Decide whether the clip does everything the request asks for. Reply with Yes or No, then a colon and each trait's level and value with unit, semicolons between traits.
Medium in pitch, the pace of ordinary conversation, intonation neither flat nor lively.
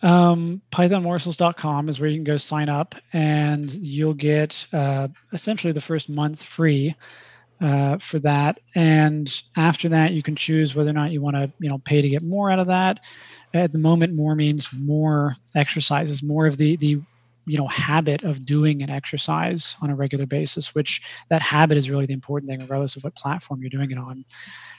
No: medium, 150 Hz; average, 195 wpm; narrow, 2.1 semitones